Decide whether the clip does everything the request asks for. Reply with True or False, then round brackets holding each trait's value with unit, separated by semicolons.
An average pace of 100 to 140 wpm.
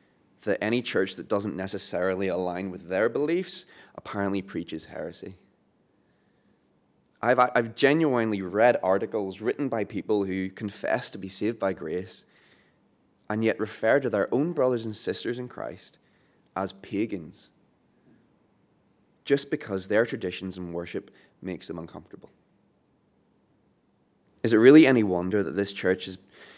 True (135 wpm)